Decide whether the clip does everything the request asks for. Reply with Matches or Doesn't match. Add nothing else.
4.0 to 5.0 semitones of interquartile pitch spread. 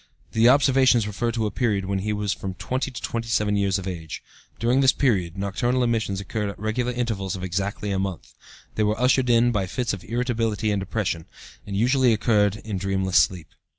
Doesn't match